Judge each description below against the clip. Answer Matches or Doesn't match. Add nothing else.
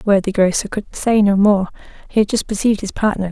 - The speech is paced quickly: Matches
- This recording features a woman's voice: Matches